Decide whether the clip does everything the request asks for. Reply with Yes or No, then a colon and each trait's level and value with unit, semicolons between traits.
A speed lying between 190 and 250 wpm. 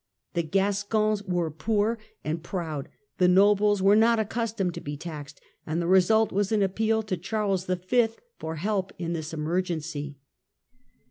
No: average, 150 wpm